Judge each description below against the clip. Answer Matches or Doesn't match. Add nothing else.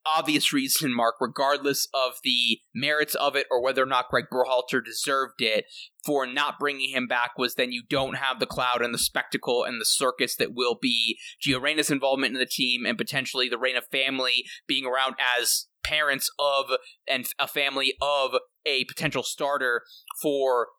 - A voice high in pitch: Doesn't match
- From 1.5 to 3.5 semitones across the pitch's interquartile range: Matches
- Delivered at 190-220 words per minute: Doesn't match